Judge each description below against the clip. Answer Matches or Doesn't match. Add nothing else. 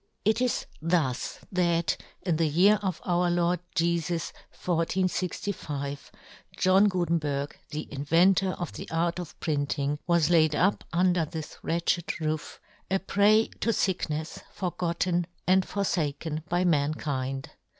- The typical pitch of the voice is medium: Matches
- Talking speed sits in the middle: Doesn't match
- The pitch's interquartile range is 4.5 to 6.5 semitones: Doesn't match